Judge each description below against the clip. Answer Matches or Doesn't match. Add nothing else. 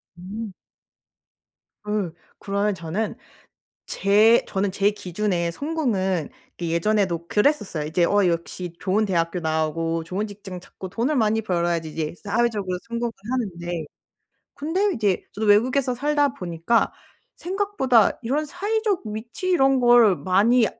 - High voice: Matches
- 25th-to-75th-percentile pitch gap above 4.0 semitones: Matches